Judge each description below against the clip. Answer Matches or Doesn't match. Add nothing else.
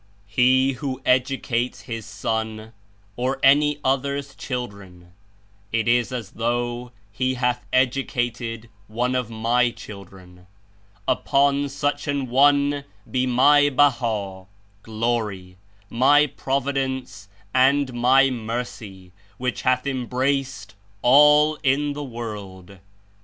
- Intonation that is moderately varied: Matches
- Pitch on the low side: Matches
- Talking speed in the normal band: Doesn't match